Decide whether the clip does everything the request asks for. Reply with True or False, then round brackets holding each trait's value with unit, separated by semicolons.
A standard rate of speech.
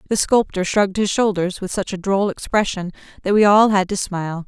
False (215 wpm)